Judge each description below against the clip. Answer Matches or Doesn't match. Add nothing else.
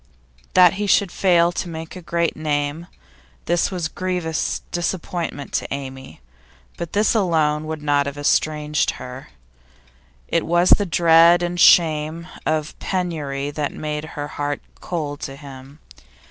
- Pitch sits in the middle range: Matches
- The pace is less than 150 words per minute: Matches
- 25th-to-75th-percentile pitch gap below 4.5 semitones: Matches